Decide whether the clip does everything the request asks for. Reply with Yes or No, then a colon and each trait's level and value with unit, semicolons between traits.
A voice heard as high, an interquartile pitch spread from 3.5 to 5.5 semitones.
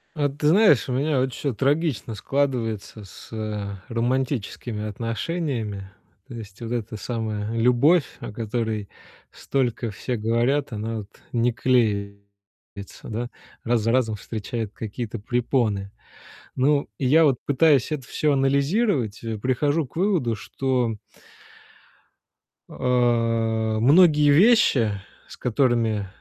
No: low, 120 Hz; average, 3.9 semitones